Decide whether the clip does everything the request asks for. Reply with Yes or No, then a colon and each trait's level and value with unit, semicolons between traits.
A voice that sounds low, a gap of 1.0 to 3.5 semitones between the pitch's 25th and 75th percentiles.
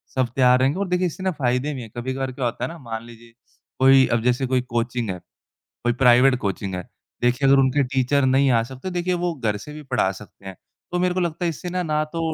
No: low, 130 Hz; average, 4.1 semitones